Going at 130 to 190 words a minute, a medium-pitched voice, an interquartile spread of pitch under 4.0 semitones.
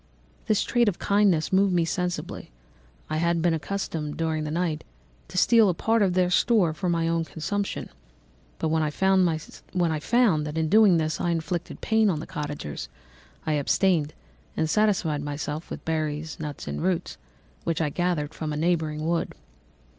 Yes: average, 170 wpm; medium, 165 Hz; average, 3.2 semitones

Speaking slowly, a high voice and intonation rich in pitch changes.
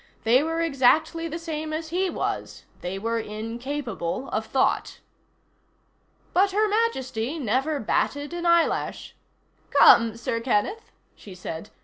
Yes: slow, 125 wpm; very high, 275 Hz; wide, 6.5 semitones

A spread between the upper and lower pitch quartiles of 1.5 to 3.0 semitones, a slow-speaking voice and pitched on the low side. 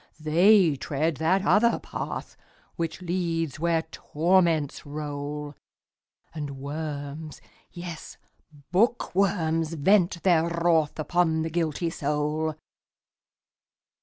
No: narrow, 2.4 semitones; slow, 75 wpm; medium, 160 Hz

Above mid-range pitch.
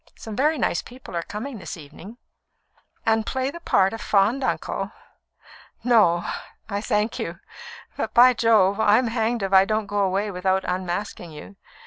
Yes: high, 210 Hz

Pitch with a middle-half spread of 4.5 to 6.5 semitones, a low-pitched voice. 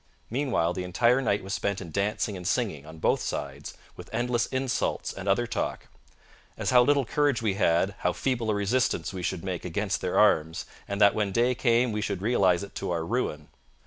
Yes: average, 4.9 semitones; low, 100 Hz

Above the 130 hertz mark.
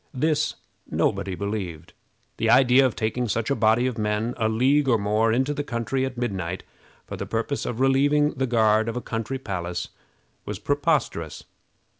No: low, 115 Hz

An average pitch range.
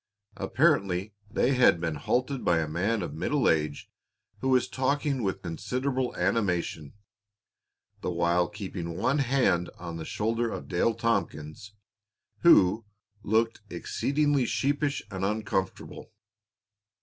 No: wide, 6.8 semitones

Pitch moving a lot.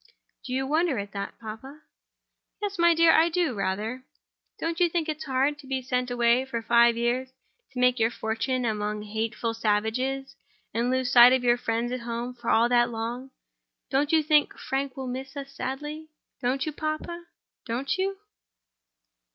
No: average, 3.8 semitones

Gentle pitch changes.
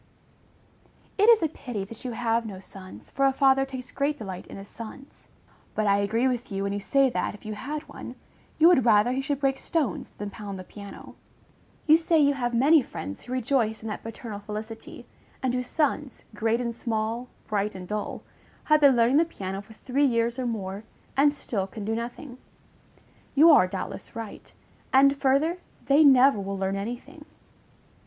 No: average, 4.7 semitones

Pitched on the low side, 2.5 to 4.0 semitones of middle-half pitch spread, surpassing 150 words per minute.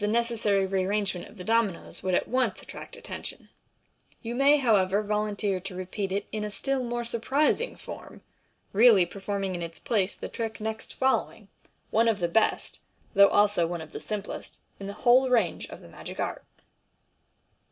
No: high, 210 Hz; average, 3.3 semitones; average, 175 wpm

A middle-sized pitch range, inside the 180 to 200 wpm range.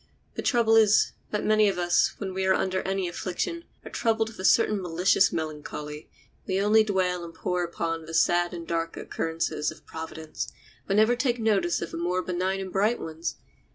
Yes: average, 4.0 semitones; average, 190 wpm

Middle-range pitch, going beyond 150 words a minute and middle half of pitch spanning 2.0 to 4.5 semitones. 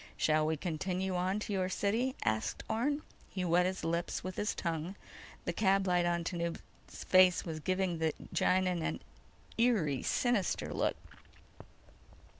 No: medium, 180 Hz; average, 145 wpm; narrow, 2.4 semitones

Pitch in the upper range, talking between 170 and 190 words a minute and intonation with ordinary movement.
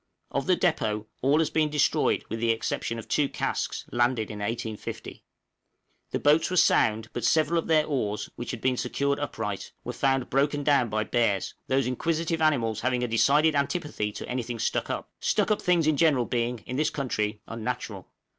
No: low, 125 Hz; average, 185 wpm; average, 4.7 semitones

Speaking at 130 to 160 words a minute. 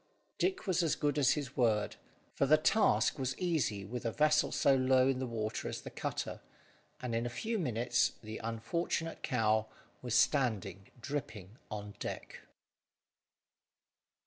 Yes: average, 150 wpm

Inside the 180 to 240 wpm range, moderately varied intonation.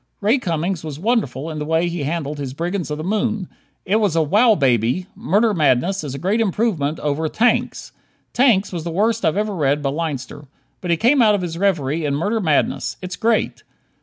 No: fast, 205 wpm; wide, 5.7 semitones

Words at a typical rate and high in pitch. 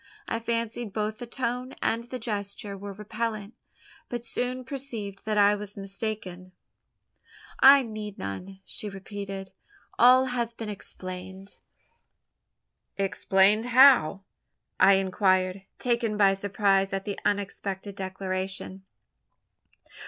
No: slow, 110 wpm; high, 205 Hz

